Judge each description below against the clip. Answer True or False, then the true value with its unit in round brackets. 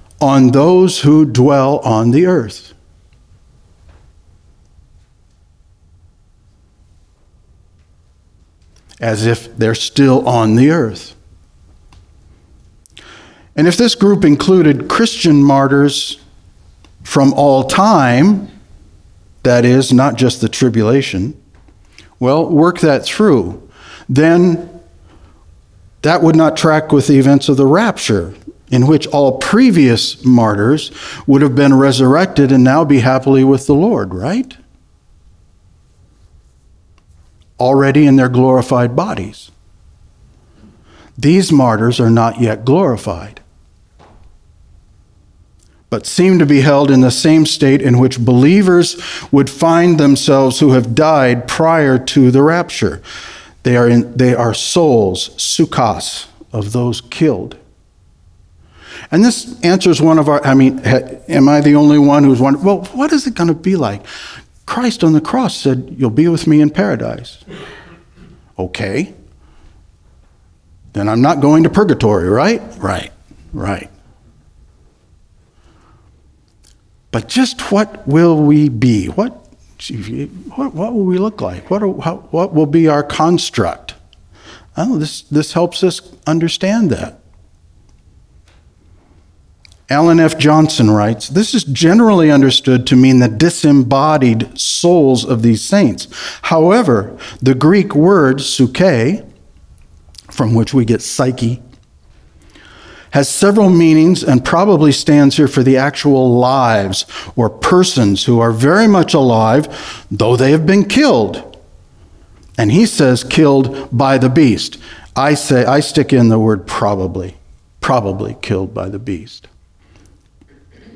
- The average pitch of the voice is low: True (130 Hz)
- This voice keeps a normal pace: False (120 wpm)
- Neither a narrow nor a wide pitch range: False (8.4 semitones)